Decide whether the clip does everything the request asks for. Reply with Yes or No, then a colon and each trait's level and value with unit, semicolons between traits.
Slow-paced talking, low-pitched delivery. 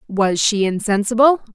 No: slow, 115 wpm; high, 220 Hz